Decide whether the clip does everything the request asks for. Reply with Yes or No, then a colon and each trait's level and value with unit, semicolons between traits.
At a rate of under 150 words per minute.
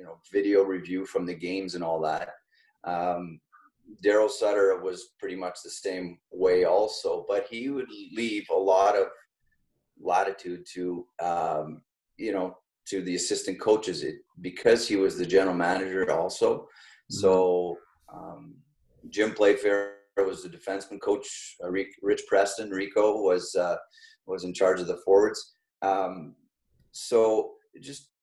Yes: average, 140 wpm